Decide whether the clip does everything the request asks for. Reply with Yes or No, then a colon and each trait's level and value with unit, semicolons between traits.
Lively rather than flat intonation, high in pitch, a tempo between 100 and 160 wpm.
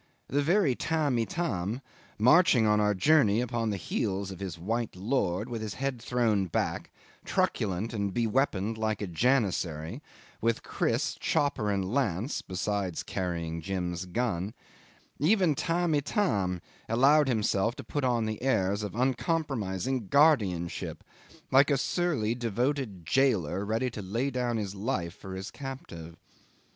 No: wide, 5.7 semitones; low, 110 Hz; average, 140 wpm